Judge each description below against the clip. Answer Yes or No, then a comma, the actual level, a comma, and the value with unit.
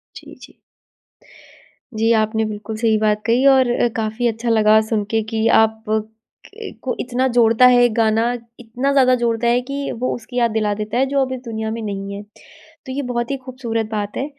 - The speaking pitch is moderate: No, high, 225 Hz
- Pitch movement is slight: Yes, narrow, 2.2 semitones